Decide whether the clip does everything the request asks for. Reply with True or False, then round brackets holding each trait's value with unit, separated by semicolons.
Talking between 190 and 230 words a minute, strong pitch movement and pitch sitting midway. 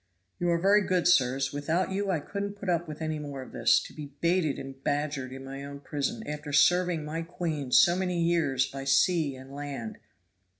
False (205 wpm; 4.3 semitones; 150 Hz)